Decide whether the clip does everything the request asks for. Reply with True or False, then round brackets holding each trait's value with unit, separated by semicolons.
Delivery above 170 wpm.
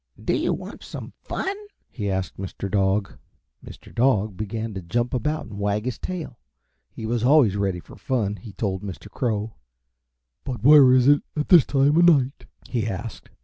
True (180 wpm)